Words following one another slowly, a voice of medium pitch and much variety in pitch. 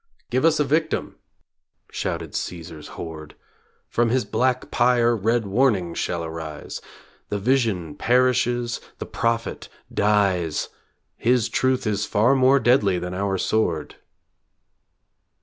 No: slow, 115 wpm; low, 110 Hz; wide, 5.7 semitones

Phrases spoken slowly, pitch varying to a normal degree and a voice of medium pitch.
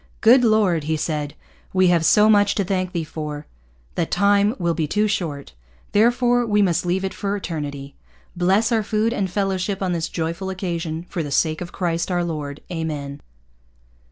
No: average, 180 wpm; average, 4.1 semitones; medium, 180 Hz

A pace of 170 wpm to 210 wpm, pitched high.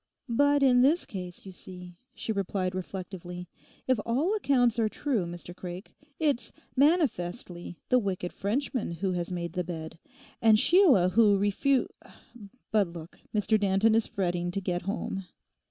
No: average, 150 wpm; high, 195 Hz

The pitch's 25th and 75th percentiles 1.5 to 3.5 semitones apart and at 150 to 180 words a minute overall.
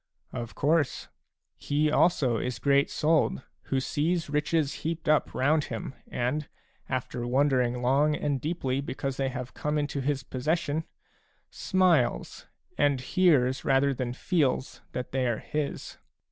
No: average, 3.0 semitones; average, 140 wpm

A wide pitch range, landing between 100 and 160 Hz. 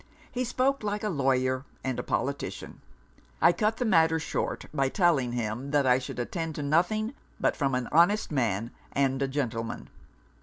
Yes: wide, 5.9 semitones; medium, 140 Hz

